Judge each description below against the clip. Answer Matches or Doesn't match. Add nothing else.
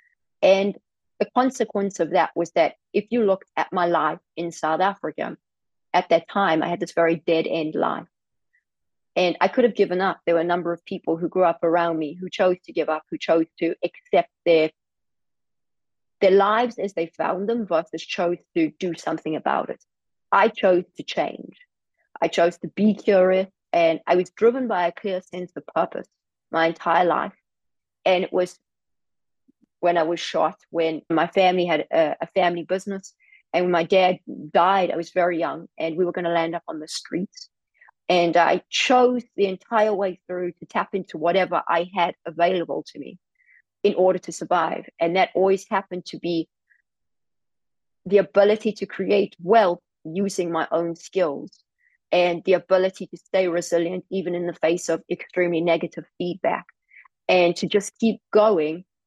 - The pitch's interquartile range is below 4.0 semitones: Matches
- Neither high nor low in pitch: Matches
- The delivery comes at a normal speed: Matches